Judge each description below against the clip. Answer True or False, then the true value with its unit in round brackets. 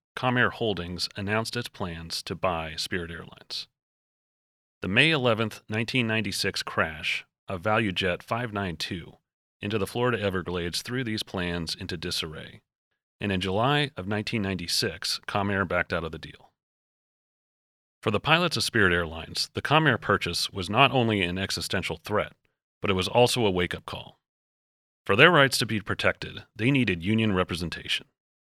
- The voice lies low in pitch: True (100 Hz)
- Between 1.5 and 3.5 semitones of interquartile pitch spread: False (4.2 semitones)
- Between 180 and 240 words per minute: False (150 wpm)